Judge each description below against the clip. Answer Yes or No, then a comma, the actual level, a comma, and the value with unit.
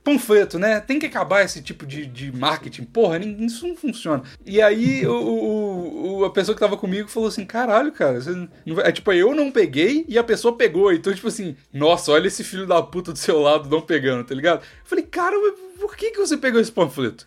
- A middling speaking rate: No, fast, 225 wpm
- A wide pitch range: Yes, wide, 8.2 semitones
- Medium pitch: No, high, 210 Hz